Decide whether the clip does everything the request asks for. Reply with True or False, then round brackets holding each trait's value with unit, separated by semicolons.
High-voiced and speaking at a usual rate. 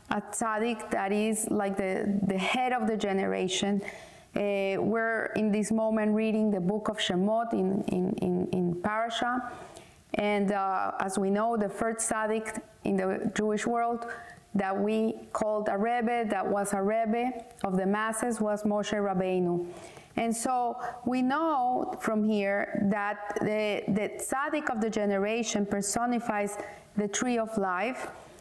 True (215 Hz; 150 wpm)